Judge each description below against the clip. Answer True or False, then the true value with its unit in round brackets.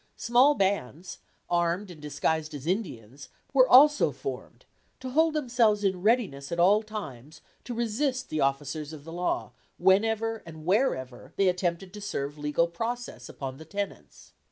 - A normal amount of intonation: False (6.8 semitones)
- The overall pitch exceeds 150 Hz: True (185 Hz)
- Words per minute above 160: False (155 wpm)